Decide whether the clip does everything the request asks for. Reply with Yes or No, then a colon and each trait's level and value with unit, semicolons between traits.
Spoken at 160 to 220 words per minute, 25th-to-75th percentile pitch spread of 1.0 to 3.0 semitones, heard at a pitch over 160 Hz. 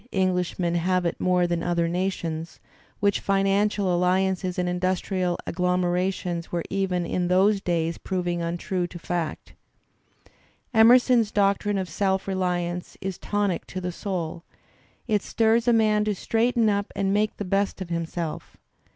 No: average, 145 wpm; narrow, 2.4 semitones; medium, 185 Hz